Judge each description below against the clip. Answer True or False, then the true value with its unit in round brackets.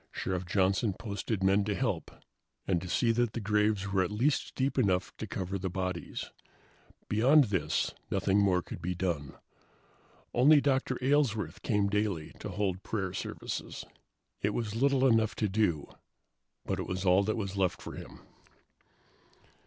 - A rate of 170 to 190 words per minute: False (155 wpm)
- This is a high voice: False (100 Hz)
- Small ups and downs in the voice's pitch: False (3.4 semitones)